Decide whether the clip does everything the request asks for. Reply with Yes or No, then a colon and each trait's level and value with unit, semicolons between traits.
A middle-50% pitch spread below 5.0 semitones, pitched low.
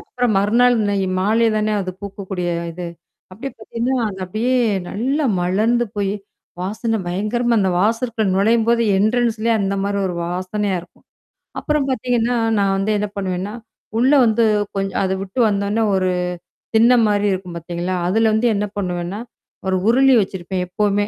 No: average, 3.5 semitones; high, 205 Hz